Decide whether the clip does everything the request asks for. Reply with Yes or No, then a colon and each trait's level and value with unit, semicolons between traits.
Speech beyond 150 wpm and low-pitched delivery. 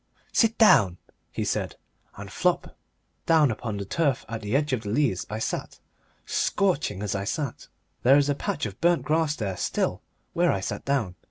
Yes: average, 185 wpm; low, 130 Hz